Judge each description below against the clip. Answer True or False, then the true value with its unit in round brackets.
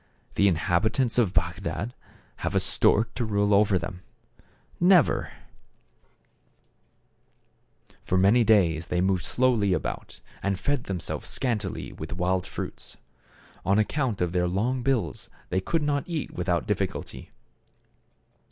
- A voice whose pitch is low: True (100 Hz)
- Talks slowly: True (125 wpm)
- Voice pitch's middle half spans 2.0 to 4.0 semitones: False (5.1 semitones)